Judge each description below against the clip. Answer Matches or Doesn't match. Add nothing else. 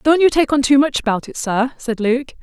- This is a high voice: Matches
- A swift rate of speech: Matches